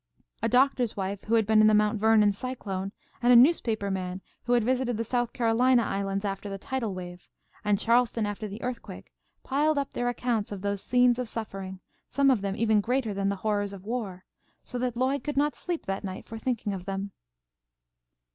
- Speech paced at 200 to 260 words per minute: Yes, fast, 205 wpm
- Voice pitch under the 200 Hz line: No, high, 220 Hz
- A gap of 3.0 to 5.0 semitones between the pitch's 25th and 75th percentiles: Yes, average, 3.8 semitones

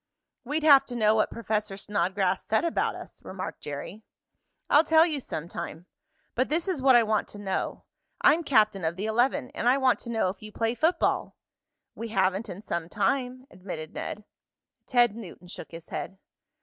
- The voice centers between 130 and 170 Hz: No, high, 220 Hz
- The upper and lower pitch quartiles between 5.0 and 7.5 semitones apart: Yes, average, 5.3 semitones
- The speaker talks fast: No, average, 185 wpm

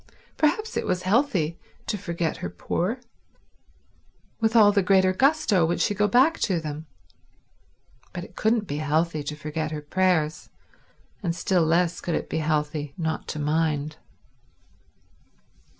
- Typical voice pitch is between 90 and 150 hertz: No, medium, 170 Hz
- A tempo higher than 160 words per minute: No, average, 145 wpm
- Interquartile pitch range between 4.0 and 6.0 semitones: Yes, average, 4.9 semitones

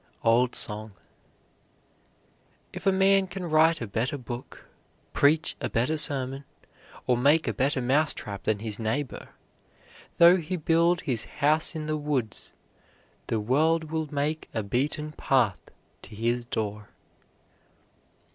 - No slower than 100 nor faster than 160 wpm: Yes, slow, 135 wpm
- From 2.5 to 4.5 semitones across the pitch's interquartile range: No, wide, 5.5 semitones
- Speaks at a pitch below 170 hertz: Yes, medium, 140 Hz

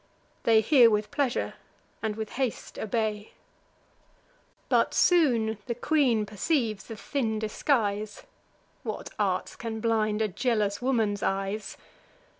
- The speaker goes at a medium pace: No, slow, 115 wpm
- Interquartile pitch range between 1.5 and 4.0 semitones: Yes, narrow, 2.5 semitones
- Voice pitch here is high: Yes, high, 220 Hz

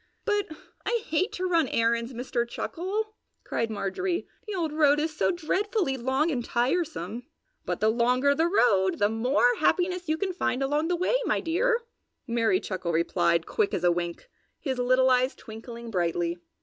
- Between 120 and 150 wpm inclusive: No, average, 170 wpm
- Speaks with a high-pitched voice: Yes, very high, 265 Hz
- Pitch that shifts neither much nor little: No, wide, 7.3 semitones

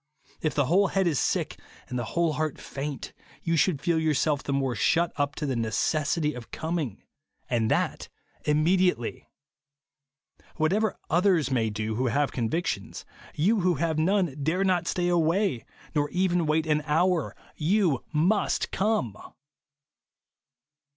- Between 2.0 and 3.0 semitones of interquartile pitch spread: No, average, 4.2 semitones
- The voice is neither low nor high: Yes, medium, 155 Hz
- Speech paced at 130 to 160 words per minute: Yes, average, 150 wpm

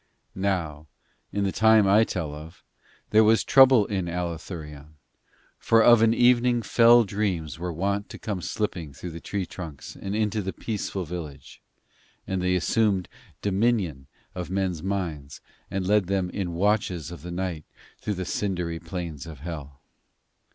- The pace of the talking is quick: No, average, 155 wpm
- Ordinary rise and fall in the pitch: Yes, average, 3.9 semitones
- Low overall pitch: Yes, very low, 95 Hz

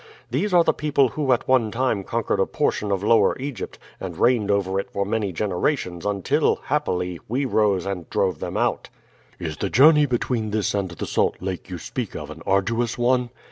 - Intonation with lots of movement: No, average, 4.7 semitones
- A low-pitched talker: Yes, low, 105 Hz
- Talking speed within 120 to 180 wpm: No, average, 195 wpm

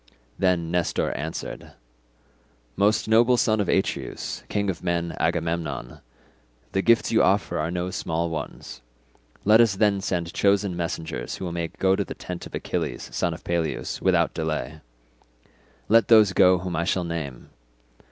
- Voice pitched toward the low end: Yes, very low, 90 Hz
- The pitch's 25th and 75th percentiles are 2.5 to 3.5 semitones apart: Yes, average, 3.1 semitones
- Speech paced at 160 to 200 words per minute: No, average, 150 wpm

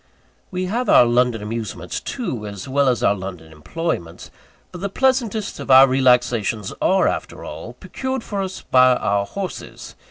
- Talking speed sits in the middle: Yes, average, 160 wpm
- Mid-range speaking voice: No, low, 130 Hz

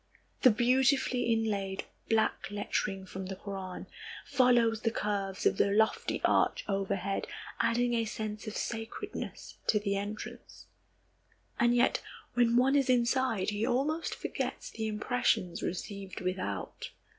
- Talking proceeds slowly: Yes, slow, 130 wpm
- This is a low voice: No, high, 220 Hz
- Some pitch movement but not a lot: Yes, average, 3.5 semitones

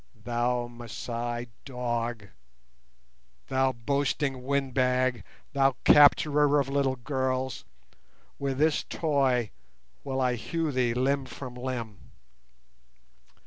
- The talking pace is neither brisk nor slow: No, slow, 95 wpm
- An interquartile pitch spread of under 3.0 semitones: Yes, narrow, 2.4 semitones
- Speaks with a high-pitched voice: No, low, 130 Hz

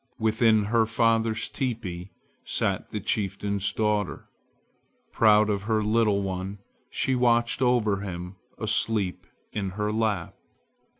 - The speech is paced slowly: Yes, slow, 115 wpm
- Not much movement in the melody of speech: Yes, narrow, 2.2 semitones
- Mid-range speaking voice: No, low, 105 Hz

